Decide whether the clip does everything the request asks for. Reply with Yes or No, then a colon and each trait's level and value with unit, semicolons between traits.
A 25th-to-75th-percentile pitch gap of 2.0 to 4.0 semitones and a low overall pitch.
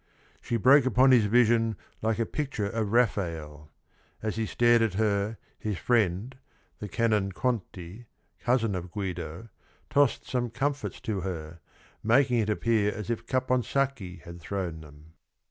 No: average, 4.6 semitones; low, 110 Hz